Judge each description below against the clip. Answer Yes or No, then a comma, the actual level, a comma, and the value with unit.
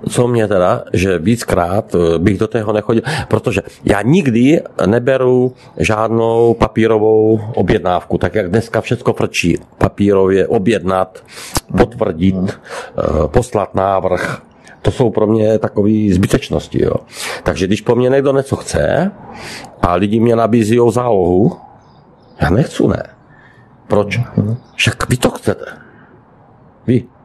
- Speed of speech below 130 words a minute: Yes, average, 120 wpm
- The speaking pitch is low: Yes, low, 110 Hz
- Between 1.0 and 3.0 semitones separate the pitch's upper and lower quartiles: No, average, 3.4 semitones